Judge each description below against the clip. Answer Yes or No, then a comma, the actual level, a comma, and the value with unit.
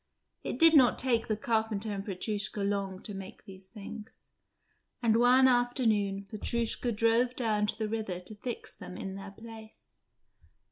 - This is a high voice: Yes, high, 220 Hz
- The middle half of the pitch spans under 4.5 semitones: Yes, average, 2.8 semitones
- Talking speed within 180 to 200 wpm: No, average, 155 wpm